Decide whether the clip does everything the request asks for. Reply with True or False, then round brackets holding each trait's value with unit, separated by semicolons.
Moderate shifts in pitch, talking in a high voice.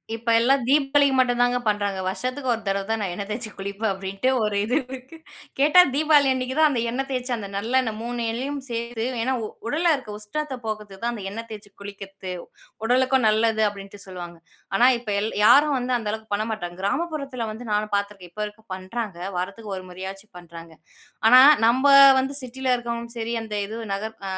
True (4.1 semitones; 225 Hz)